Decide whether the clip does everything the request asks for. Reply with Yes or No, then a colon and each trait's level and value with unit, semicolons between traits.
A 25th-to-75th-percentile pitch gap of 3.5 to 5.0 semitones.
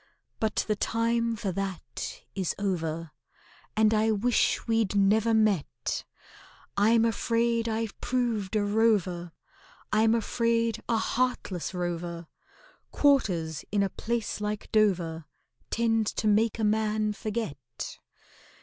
No: average, 3.0 semitones